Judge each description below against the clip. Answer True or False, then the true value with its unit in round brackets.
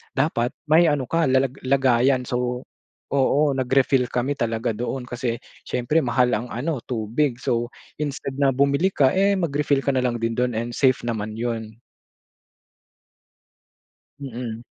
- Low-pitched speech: True (130 Hz)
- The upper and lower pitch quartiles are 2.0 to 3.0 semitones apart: True (2.6 semitones)